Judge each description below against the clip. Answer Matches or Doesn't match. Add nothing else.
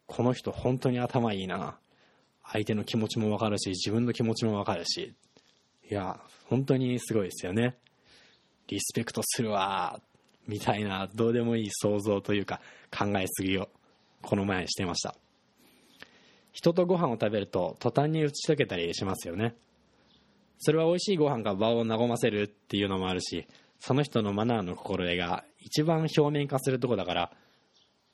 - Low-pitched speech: Matches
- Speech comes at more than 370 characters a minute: Doesn't match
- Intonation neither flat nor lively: Matches